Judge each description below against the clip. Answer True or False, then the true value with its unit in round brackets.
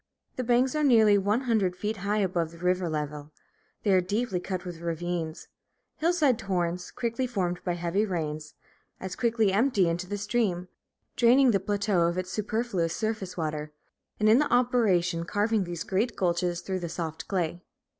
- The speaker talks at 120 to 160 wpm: False (170 wpm)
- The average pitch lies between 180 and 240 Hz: True (190 Hz)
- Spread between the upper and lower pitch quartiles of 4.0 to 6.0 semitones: True (4.4 semitones)